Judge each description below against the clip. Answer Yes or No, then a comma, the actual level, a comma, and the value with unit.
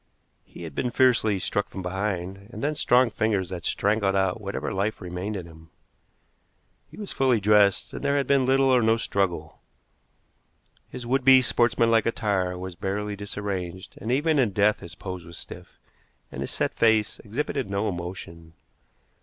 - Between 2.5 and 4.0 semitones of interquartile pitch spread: No, average, 4.4 semitones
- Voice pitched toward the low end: Yes, low, 105 Hz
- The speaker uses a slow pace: No, average, 170 wpm